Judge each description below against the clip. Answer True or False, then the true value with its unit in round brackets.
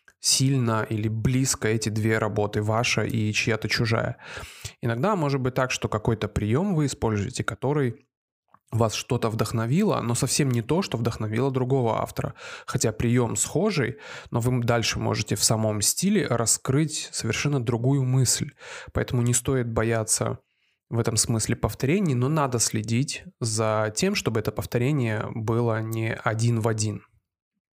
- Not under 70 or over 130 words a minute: False (145 wpm)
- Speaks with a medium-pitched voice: False (120 Hz)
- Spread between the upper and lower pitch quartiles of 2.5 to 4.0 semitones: True (3.3 semitones)